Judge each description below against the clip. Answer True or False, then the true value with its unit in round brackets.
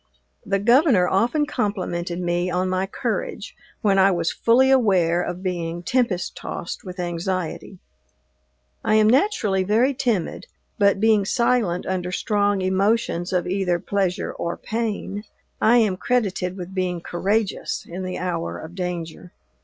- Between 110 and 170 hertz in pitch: False (190 Hz)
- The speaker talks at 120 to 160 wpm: True (140 wpm)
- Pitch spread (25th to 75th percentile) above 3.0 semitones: True (3.4 semitones)